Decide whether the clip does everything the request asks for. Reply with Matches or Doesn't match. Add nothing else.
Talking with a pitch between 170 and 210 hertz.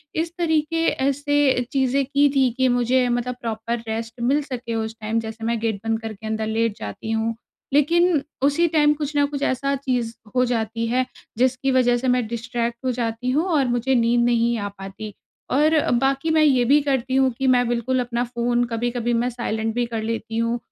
Doesn't match